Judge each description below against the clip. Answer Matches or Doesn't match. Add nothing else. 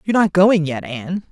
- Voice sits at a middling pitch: Matches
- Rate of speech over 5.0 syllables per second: Matches